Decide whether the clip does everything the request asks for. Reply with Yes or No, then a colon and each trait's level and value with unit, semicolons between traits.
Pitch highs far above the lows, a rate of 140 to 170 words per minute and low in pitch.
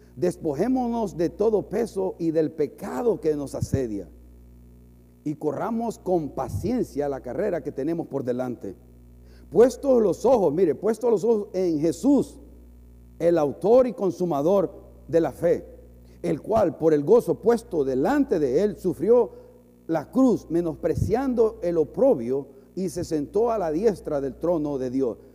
No: wide, 8.4 semitones; average, 145 wpm; medium, 165 Hz